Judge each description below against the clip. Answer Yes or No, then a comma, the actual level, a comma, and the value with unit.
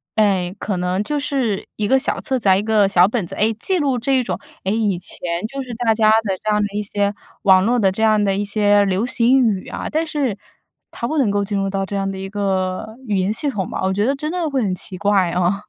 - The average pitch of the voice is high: Yes, high, 205 Hz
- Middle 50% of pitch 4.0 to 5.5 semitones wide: No, average, 3.5 semitones